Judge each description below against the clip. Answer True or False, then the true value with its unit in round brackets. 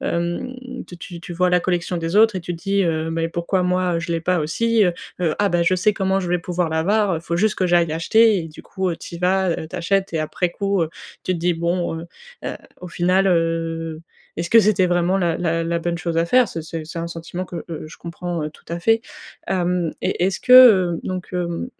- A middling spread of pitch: False (2.1 semitones)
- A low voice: False (175 Hz)